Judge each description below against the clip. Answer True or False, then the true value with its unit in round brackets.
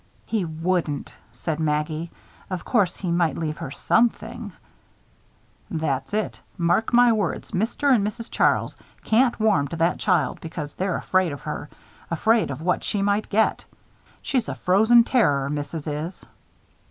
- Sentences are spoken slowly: False (150 wpm)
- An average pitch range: False (6.0 semitones)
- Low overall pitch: False (180 Hz)